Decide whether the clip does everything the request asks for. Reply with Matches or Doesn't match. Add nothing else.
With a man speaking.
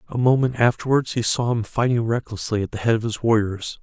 Matches